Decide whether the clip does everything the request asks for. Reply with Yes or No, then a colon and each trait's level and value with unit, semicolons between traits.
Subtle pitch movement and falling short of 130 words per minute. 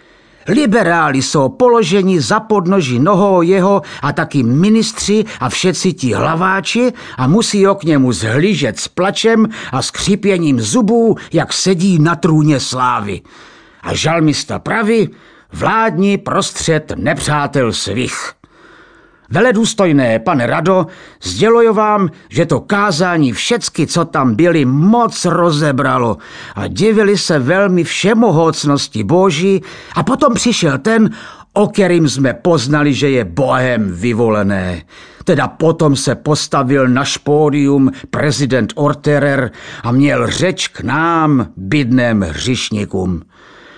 No: wide, 6.3 semitones; slow, 115 wpm